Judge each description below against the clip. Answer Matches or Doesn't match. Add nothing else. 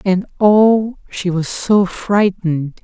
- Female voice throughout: Doesn't match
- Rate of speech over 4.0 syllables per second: Doesn't match